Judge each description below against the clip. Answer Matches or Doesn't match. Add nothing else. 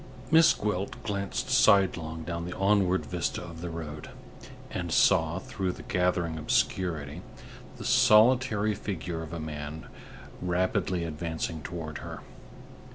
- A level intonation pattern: Doesn't match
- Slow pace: Matches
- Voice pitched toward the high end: Doesn't match